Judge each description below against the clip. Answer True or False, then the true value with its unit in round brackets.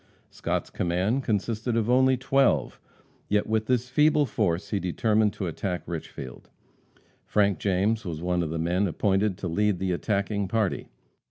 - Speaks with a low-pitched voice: True (100 Hz)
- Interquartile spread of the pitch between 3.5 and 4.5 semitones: True (3.8 semitones)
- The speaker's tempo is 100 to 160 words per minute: True (155 wpm)